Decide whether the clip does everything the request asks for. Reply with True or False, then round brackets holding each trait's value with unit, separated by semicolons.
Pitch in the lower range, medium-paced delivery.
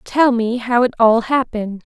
False (235 Hz; 185 wpm)